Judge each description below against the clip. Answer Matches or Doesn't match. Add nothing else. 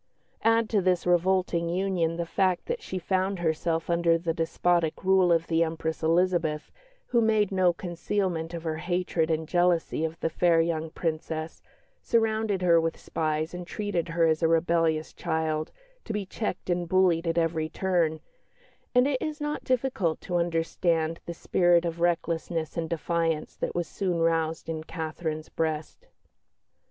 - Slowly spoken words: Doesn't match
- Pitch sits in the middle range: Matches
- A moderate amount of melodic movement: Doesn't match